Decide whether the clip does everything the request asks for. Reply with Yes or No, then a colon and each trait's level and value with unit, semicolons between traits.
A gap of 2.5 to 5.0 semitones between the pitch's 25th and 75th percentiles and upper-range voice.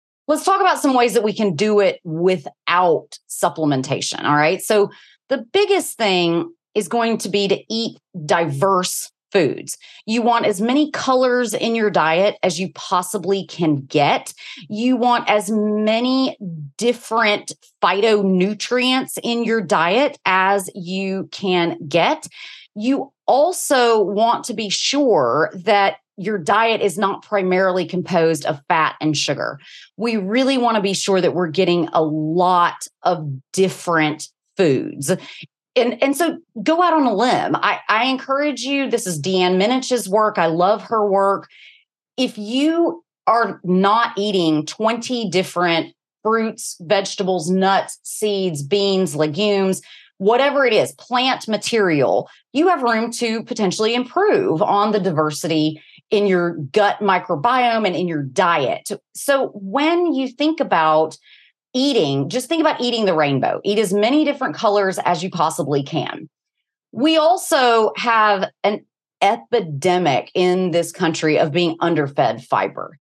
No: wide, 5.4 semitones; high, 205 Hz